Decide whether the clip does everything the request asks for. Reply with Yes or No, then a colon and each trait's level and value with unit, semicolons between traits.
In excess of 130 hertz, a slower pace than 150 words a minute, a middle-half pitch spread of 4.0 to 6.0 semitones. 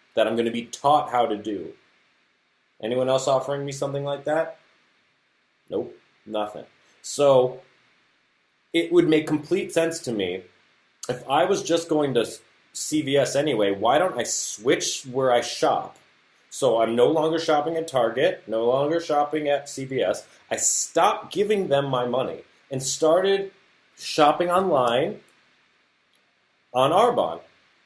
Yes: medium, 140 Hz; average, 140 wpm; average, 4.3 semitones